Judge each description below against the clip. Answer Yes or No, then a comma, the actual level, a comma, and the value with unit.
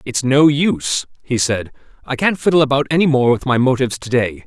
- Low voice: Yes, low, 130 Hz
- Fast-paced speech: Yes, fast, 215 wpm